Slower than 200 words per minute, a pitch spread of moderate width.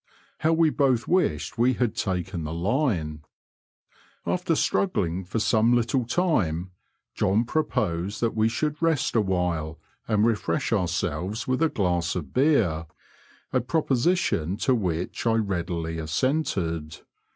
No: slow, 135 wpm; wide, 7.2 semitones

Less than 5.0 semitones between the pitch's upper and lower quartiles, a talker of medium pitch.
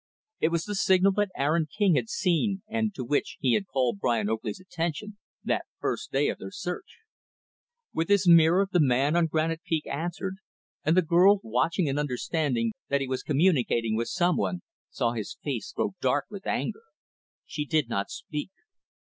No: wide, 5.6 semitones; medium, 160 Hz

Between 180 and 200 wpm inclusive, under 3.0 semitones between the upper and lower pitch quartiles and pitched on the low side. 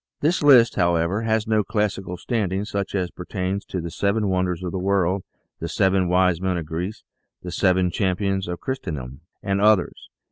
Yes: average, 190 wpm; narrow, 2.4 semitones; very low, 95 Hz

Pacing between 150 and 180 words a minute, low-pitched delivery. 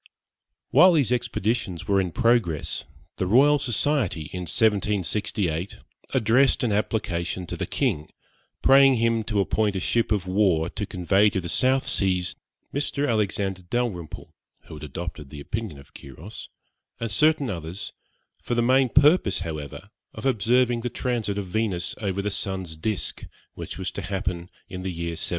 Yes: average, 160 wpm; low, 100 Hz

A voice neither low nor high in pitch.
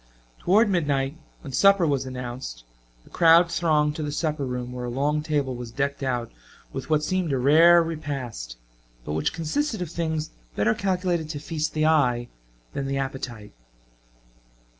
Yes: medium, 150 Hz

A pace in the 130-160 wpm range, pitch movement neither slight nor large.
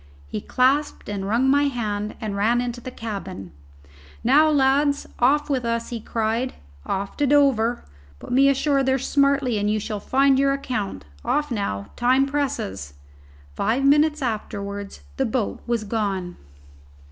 Yes: average, 150 wpm; average, 5.0 semitones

